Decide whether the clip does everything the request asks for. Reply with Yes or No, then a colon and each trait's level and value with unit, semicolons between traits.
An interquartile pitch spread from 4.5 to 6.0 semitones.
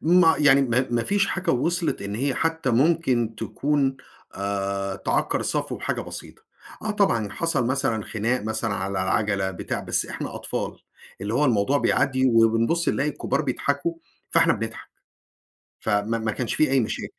Yes: average, 5.3 semitones